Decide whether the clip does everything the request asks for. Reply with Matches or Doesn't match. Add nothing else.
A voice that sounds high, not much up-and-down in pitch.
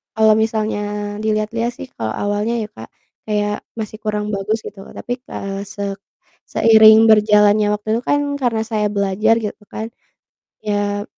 Matches